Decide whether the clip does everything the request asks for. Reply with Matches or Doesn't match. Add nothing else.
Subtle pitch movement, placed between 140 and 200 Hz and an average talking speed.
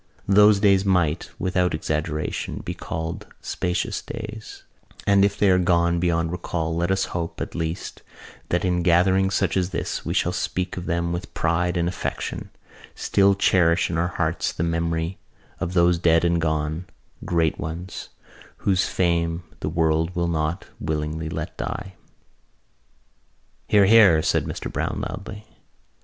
Doesn't match